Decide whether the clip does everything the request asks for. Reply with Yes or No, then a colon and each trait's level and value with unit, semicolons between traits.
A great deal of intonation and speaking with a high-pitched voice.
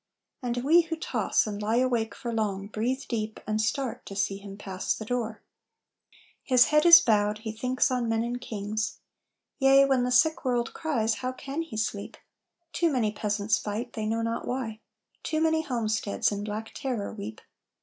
No: average, 3.2 semitones; high, 230 Hz